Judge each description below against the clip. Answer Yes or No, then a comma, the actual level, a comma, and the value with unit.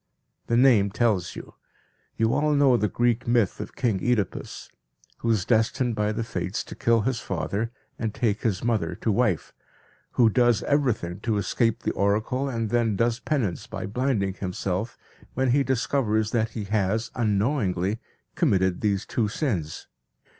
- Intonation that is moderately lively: Yes, average, 3.3 semitones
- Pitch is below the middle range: Yes, low, 110 Hz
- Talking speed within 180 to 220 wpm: No, average, 160 wpm